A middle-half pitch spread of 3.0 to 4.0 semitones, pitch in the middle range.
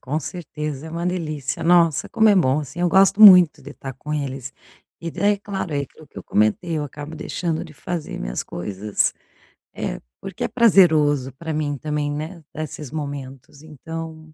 Yes: average, 3.4 semitones; medium, 155 Hz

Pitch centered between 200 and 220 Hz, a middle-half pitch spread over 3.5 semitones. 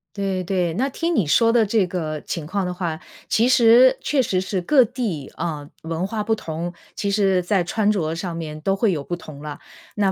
No: high, 190 Hz; average, 4.7 semitones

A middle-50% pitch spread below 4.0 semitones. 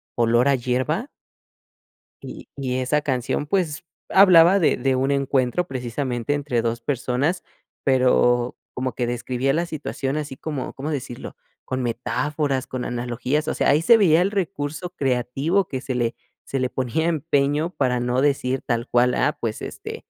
Yes: average, 3.4 semitones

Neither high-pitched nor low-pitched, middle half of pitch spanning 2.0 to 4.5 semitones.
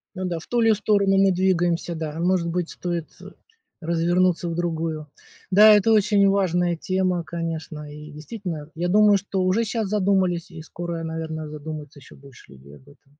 Yes: medium, 175 Hz; average, 3.2 semitones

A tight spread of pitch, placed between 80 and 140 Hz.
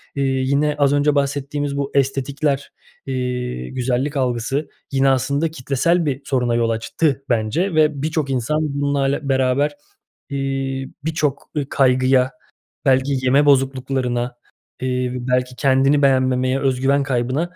Yes: narrow, 1.9 semitones; low, 135 Hz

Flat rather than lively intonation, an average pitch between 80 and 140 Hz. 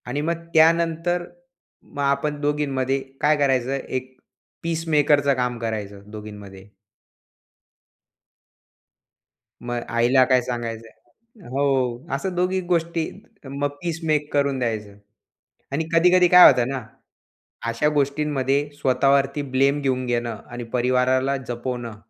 No: average, 3.5 semitones; low, 135 Hz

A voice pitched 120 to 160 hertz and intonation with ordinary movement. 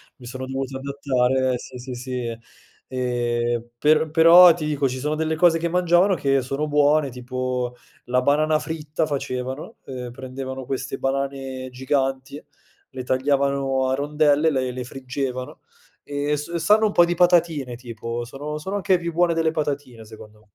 Yes: low, 135 Hz; average, 3.2 semitones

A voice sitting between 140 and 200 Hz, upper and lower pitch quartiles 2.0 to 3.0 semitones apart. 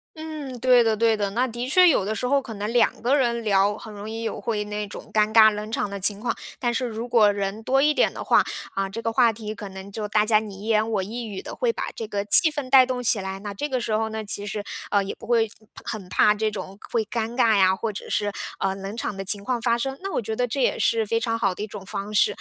No: high, 220 Hz; average, 2.7 semitones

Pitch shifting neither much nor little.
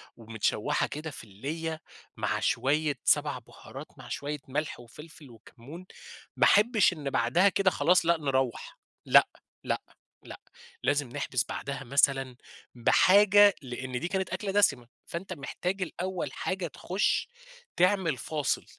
No: wide, 5.7 semitones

